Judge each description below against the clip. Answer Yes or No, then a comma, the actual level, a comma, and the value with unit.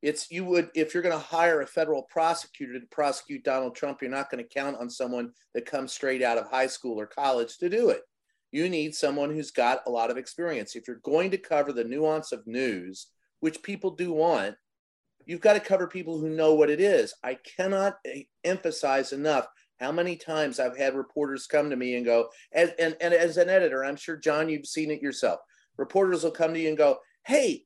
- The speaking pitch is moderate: Yes, medium, 155 Hz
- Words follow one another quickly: Yes, fast, 220 wpm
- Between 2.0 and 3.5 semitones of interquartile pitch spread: No, average, 4.1 semitones